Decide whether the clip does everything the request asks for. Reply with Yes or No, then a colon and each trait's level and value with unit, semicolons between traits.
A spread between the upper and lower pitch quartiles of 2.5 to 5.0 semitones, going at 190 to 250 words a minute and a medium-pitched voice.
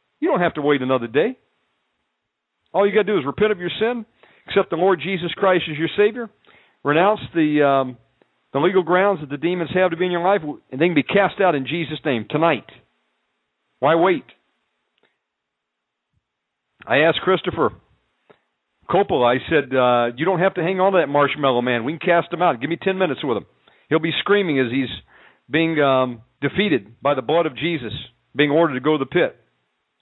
No: wide, 5.5 semitones; average, 200 wpm; medium, 165 Hz